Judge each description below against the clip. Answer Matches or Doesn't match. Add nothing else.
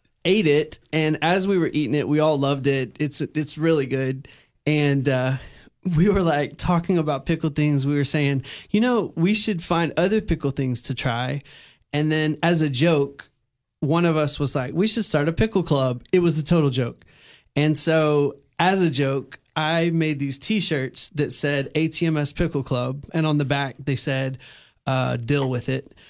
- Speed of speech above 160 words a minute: Matches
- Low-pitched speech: Doesn't match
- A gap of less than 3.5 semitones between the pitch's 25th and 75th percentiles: Matches